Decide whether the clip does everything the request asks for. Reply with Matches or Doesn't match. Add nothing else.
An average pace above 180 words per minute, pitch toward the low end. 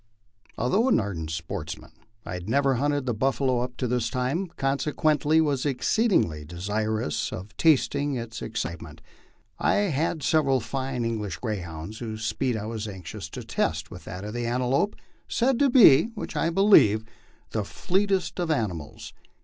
Doesn't match